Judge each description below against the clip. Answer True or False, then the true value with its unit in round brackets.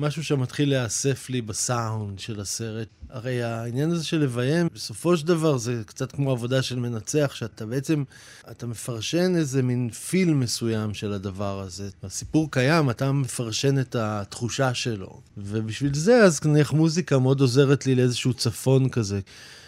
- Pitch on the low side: True (125 Hz)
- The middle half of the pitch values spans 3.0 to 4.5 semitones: True (4.2 semitones)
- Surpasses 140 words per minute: True (150 wpm)